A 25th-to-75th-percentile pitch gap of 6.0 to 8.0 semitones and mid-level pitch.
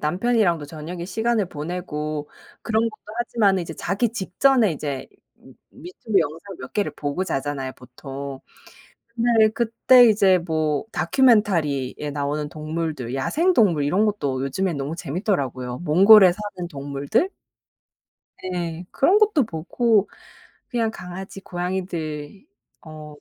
Yes: wide, 6.3 semitones; medium, 175 Hz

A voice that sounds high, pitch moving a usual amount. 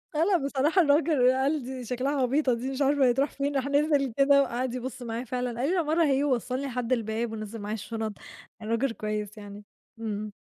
Yes: very high, 255 Hz; average, 3.6 semitones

